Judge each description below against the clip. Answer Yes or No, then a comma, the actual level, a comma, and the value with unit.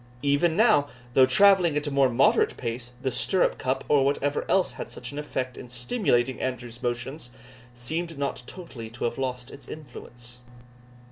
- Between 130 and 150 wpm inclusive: No, average, 165 wpm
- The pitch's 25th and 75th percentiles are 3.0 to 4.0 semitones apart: Yes, average, 3.4 semitones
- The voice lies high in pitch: No, low, 135 Hz